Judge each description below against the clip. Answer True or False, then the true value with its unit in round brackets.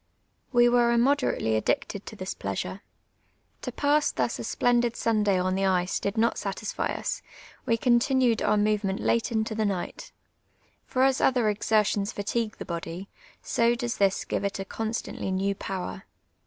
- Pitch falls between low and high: False (215 Hz)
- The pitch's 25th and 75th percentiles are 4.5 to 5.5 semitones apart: False (3.5 semitones)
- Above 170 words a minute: False (160 wpm)